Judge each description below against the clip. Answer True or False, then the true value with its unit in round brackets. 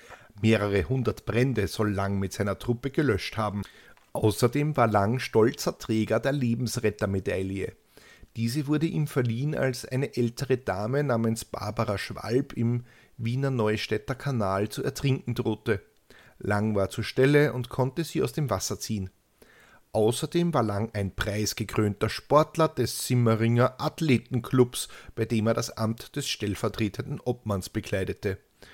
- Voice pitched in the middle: False (115 Hz)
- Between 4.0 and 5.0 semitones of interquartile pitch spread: False (3.6 semitones)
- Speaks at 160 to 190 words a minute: False (135 wpm)